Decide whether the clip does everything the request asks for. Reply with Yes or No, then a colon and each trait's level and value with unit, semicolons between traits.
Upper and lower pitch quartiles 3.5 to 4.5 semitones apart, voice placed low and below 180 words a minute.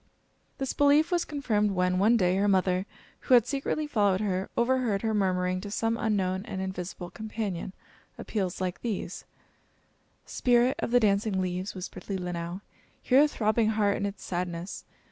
No: average, 3.9 semitones; high, 200 Hz; average, 160 wpm